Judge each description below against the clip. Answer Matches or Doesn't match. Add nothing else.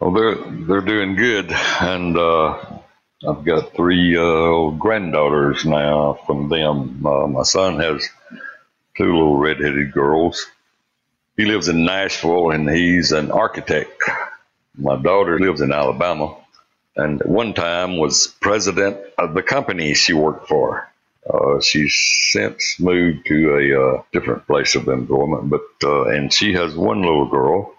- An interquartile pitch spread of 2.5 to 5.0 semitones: Matches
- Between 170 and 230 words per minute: Doesn't match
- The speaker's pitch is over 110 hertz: Doesn't match